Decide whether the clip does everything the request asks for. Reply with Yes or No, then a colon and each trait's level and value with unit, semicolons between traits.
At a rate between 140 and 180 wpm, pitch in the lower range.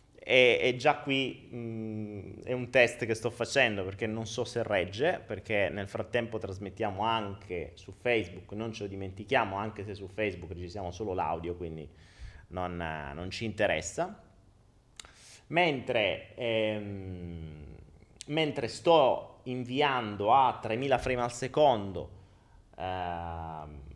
No: average, 125 wpm; low, 105 Hz